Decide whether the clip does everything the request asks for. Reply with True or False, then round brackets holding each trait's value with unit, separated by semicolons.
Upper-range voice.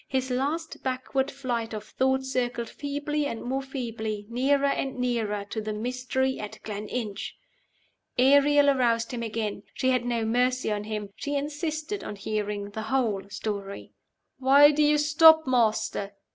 True (250 Hz)